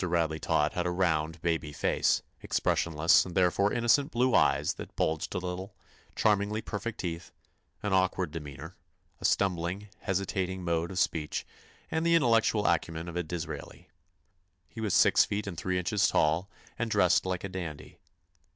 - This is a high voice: No, very low, 90 Hz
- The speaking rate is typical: Yes, average, 160 wpm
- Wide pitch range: No, average, 3.4 semitones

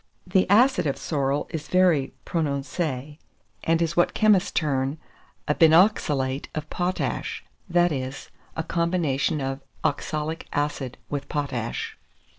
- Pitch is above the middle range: No, medium, 150 Hz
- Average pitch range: Yes, average, 3.9 semitones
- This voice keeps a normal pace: No, slow, 120 wpm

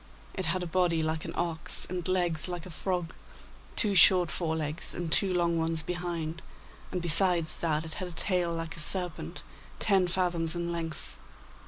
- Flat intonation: Yes, narrow, 1.8 semitones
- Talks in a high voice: No, medium, 170 Hz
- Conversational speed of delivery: Yes, average, 180 wpm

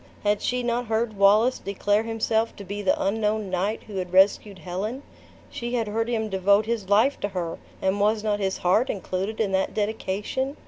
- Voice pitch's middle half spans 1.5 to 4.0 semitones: Yes, narrow, 2.5 semitones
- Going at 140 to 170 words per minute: No, average, 190 wpm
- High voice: Yes, high, 210 Hz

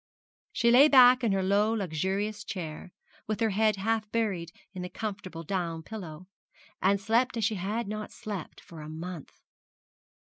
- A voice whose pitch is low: No, high, 200 Hz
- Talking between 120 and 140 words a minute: No, average, 165 wpm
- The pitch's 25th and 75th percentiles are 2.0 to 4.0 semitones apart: Yes, average, 3.5 semitones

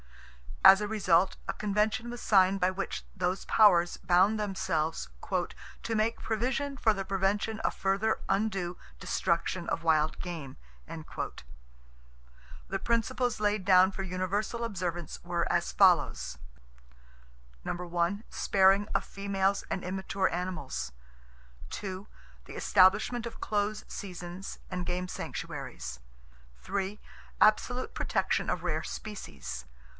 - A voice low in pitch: No, high, 190 Hz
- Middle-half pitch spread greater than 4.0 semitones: No, average, 3.4 semitones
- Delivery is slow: Yes, slow, 110 wpm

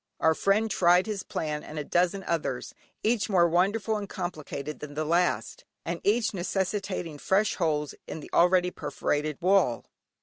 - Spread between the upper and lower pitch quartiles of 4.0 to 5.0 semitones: Yes, average, 4.4 semitones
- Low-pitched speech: No, medium, 180 Hz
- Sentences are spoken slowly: No, average, 160 wpm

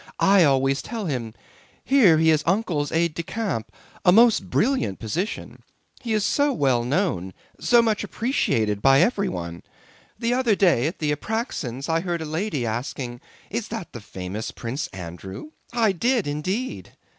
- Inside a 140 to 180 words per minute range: Yes, average, 155 wpm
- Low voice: No, medium, 160 Hz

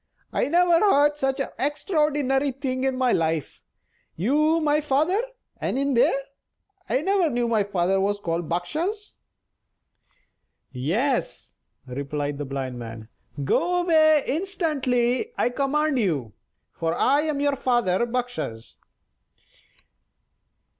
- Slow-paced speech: Yes, slow, 120 wpm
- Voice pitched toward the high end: Yes, very high, 265 Hz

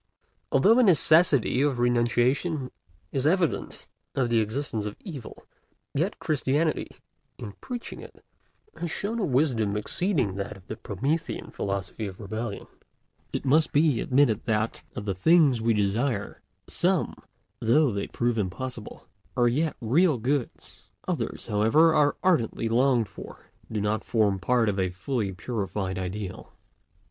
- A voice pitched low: Yes, low, 120 Hz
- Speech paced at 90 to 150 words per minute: Yes, average, 140 wpm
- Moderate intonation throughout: No, wide, 5.8 semitones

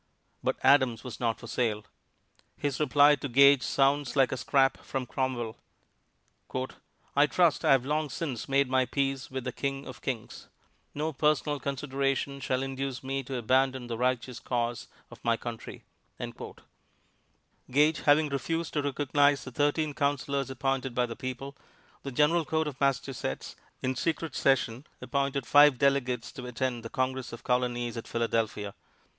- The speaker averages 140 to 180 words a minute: Yes, average, 155 wpm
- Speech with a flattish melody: Yes, narrow, 2.3 semitones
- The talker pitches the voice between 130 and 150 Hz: Yes, low, 135 Hz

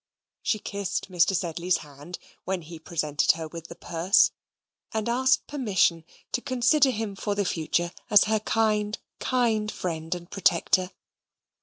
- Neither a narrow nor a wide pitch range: Yes, average, 4.4 semitones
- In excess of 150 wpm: No, average, 145 wpm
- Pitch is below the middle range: No, high, 190 Hz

